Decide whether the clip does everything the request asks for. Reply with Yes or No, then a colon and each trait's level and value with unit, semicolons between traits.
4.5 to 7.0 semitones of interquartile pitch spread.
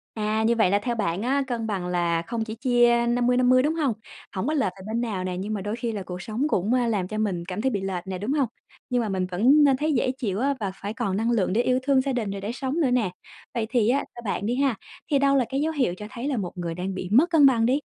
Yes: average, 4.8 semitones